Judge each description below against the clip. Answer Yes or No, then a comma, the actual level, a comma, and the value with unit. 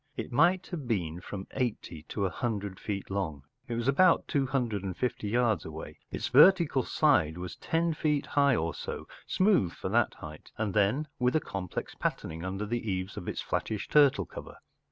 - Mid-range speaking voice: No, low, 110 Hz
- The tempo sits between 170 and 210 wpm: Yes, average, 180 wpm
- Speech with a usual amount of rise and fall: No, wide, 6.9 semitones